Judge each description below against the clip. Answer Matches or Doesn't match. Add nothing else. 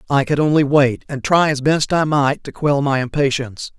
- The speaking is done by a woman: Doesn't match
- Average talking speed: Doesn't match